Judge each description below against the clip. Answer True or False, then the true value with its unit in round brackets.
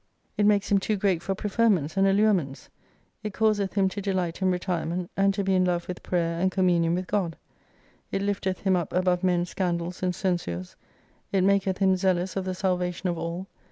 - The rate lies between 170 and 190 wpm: False (200 wpm)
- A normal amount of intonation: False (1.8 semitones)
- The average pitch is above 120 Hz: True (185 Hz)